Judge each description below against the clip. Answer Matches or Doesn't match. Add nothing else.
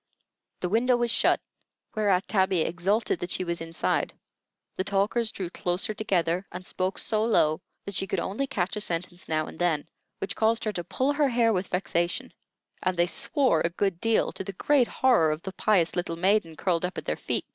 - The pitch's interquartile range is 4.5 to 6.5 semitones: Doesn't match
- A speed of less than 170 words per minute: Doesn't match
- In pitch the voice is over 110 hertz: Matches